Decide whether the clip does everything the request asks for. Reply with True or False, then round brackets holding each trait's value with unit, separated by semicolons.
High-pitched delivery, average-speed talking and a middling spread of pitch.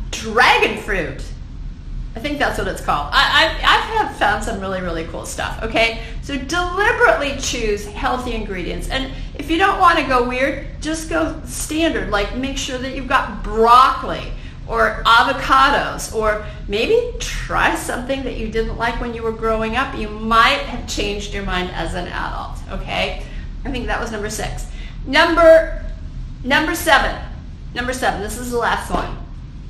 False (255 Hz; 165 wpm; 6.2 semitones)